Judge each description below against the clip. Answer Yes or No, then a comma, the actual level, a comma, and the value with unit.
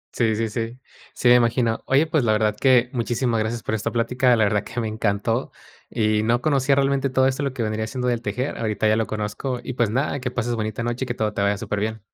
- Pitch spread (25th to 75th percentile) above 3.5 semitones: No, average, 2.7 semitones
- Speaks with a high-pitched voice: No, low, 115 Hz